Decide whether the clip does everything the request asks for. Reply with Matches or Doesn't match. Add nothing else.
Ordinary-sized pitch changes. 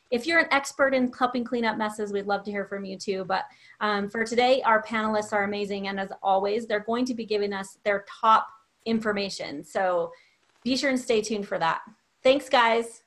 Matches